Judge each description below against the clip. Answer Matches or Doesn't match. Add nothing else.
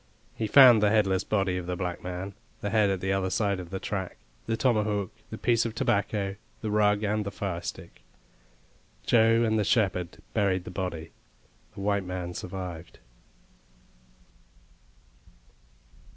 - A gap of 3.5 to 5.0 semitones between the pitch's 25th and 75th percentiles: Doesn't match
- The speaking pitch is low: Matches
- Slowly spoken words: Doesn't match